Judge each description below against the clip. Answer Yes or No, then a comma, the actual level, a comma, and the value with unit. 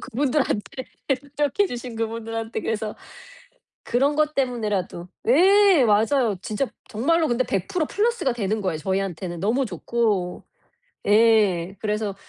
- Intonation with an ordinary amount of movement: Yes, average, 4.9 semitones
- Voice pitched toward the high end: Yes, high, 225 Hz